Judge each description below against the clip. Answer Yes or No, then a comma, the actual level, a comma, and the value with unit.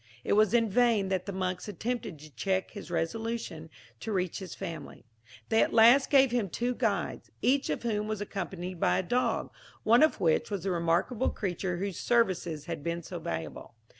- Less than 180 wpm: No, average, 190 wpm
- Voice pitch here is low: No, high, 195 Hz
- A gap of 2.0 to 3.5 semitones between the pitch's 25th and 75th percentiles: No, average, 4.9 semitones